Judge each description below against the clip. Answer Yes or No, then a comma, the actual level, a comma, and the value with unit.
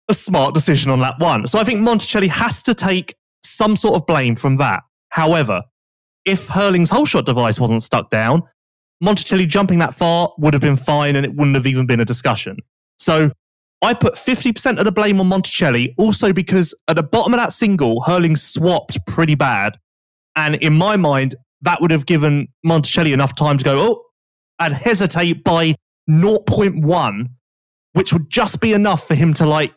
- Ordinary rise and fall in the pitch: No, wide, 5.9 semitones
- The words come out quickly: No, average, 185 wpm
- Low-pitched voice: No, medium, 165 Hz